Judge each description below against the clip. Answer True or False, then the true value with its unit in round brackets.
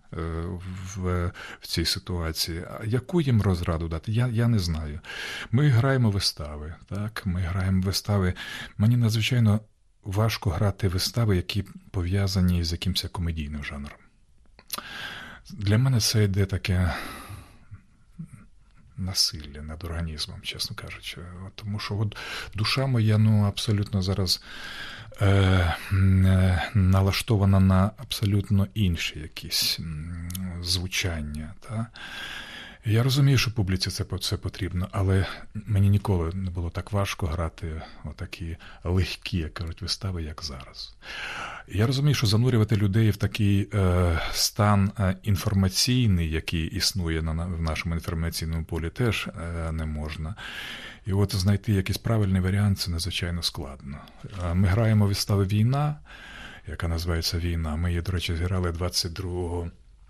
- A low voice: True (95 Hz)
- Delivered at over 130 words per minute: False (125 wpm)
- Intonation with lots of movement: False (3.5 semitones)